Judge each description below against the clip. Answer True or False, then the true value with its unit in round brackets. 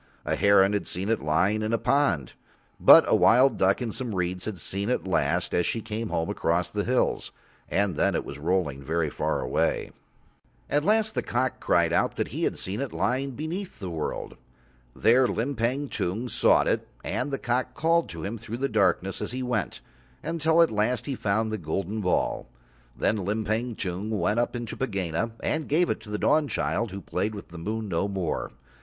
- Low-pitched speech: True (110 Hz)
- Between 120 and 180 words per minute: False (200 wpm)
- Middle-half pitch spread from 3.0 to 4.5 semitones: False (5.1 semitones)